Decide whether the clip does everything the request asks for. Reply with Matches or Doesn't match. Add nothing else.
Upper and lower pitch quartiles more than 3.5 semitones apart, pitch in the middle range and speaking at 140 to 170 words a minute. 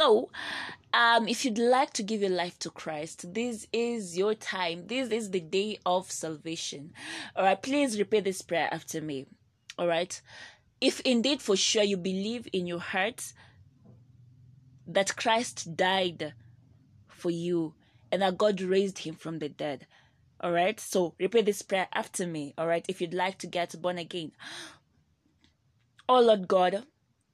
Matches